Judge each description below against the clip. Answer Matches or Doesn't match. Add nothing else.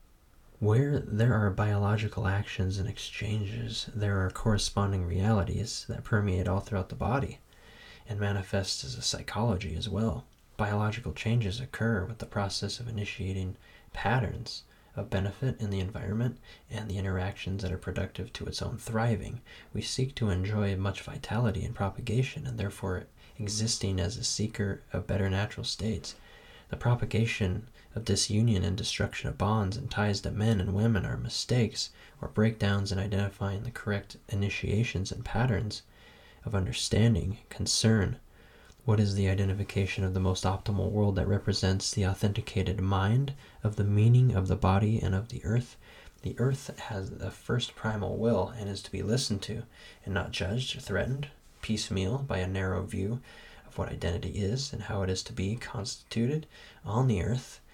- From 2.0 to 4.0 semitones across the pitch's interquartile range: Matches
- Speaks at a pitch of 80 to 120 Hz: Matches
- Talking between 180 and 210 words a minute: Doesn't match